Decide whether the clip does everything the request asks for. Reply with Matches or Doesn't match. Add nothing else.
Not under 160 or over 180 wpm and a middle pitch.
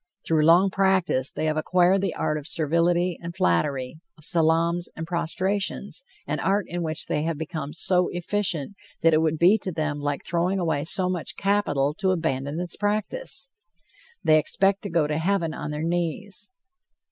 Matches